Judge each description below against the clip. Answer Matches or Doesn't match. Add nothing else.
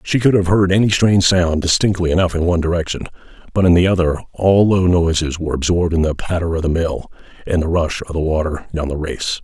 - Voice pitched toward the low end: Matches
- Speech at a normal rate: Doesn't match